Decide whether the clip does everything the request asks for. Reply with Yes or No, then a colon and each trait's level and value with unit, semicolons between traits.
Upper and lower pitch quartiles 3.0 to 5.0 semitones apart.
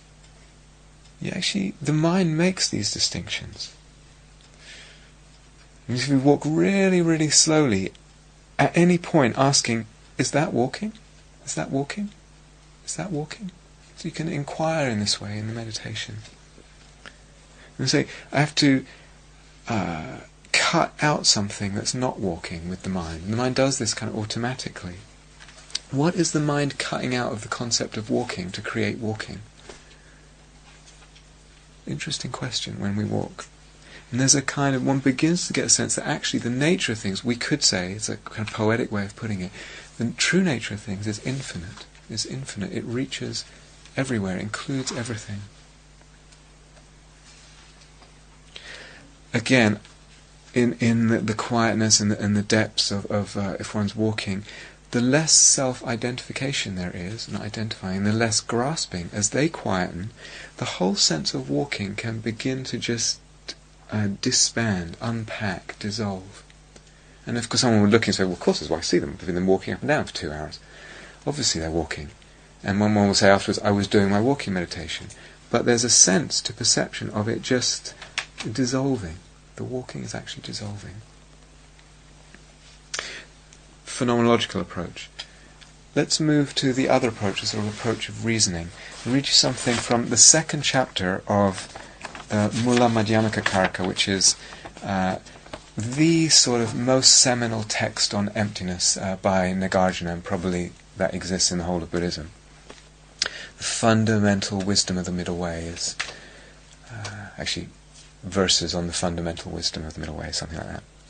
No: wide, 5.4 semitones